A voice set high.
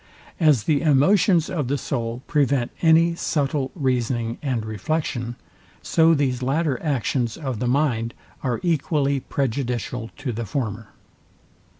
No: low, 135 Hz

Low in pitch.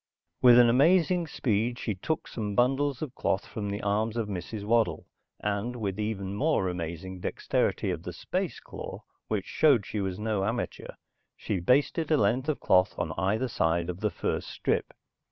Yes: low, 105 Hz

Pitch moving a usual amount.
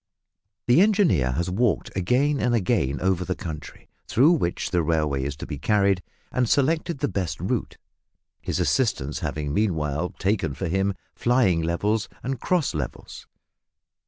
No: wide, 7.8 semitones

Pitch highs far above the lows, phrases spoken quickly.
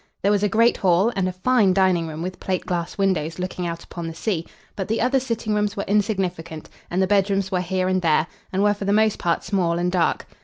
No: average, 2.8 semitones; fast, 240 wpm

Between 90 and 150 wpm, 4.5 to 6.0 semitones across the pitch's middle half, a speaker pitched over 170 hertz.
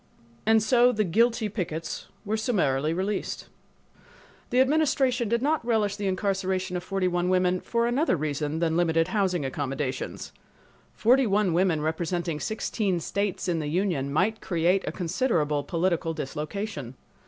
Yes: average, 140 wpm; average, 5.1 semitones; medium, 185 Hz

